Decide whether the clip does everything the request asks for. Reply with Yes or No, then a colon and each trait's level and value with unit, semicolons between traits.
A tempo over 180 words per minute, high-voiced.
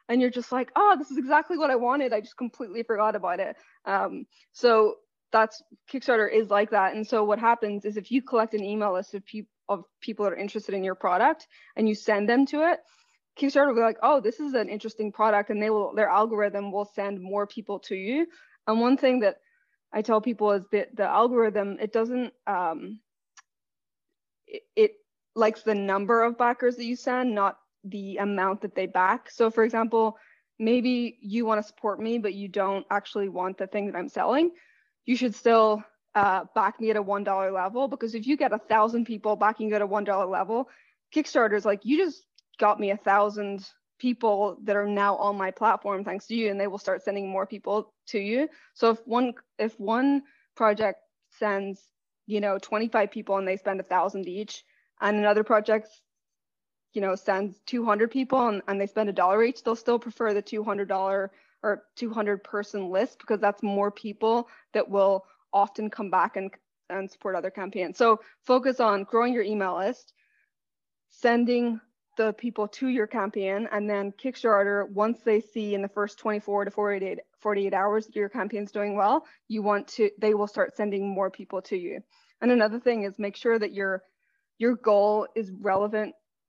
Yes: average, 195 wpm; high, 215 Hz